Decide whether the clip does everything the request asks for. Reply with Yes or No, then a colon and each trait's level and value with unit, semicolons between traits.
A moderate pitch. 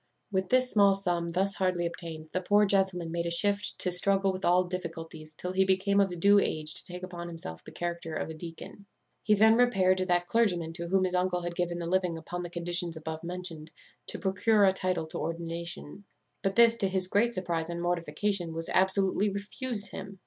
Yes: medium, 180 Hz